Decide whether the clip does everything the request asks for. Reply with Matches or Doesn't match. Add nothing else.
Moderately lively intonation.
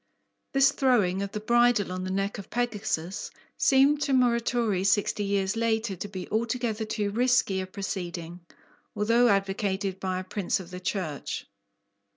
Matches